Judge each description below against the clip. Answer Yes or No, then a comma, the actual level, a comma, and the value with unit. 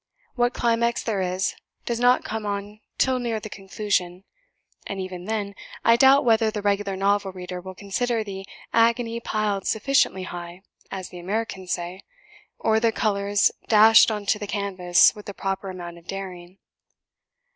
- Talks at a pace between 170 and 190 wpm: No, average, 160 wpm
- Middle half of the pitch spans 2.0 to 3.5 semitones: Yes, average, 2.9 semitones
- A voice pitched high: Yes, high, 200 Hz